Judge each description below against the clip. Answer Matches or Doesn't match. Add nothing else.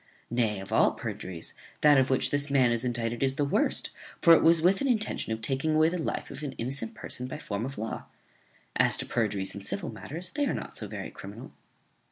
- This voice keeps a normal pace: Doesn't match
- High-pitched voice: Doesn't match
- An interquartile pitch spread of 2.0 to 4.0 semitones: Doesn't match